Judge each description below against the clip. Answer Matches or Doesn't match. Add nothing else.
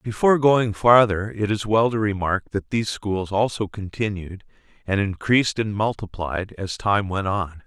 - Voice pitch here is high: Doesn't match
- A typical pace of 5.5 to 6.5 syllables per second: Doesn't match